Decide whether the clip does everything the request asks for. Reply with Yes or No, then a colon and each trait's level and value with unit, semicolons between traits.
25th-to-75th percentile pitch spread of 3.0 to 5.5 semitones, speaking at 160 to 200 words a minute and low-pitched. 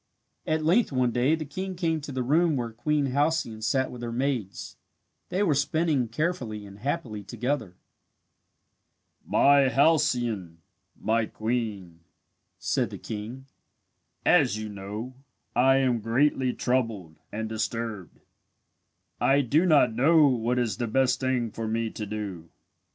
No: average, 4.5 semitones; average, 140 wpm; low, 125 Hz